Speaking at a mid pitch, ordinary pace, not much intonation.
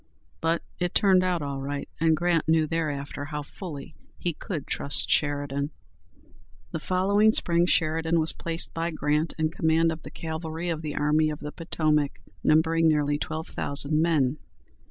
Yes: medium, 160 Hz; average, 160 wpm; narrow, 2.0 semitones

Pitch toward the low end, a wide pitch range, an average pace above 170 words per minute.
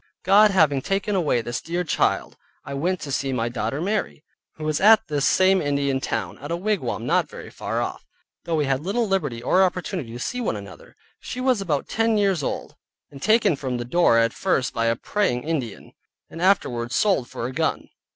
No: medium, 155 Hz; wide, 7.1 semitones; fast, 205 wpm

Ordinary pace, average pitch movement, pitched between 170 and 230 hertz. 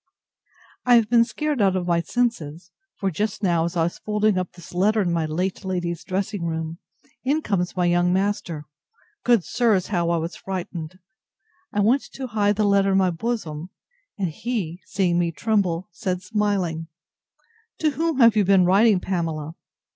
Yes: average, 175 wpm; average, 3.7 semitones; high, 190 Hz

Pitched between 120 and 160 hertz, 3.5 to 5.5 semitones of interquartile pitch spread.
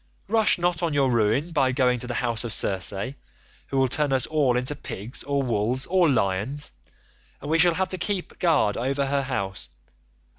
Yes: low, 135 Hz; average, 4.8 semitones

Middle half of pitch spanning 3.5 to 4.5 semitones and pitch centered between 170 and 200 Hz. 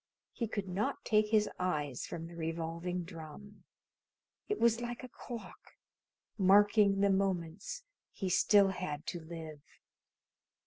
Yes: average, 4.1 semitones; high, 190 Hz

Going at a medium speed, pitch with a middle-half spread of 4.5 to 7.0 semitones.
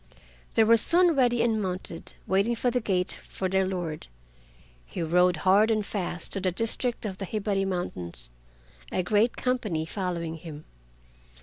No: average, 155 wpm; average, 4.1 semitones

